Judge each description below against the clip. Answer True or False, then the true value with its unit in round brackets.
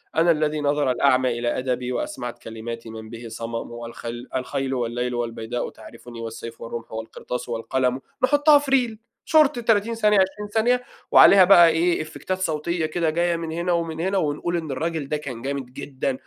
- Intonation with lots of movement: True (6.4 semitones)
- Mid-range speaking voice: True (145 Hz)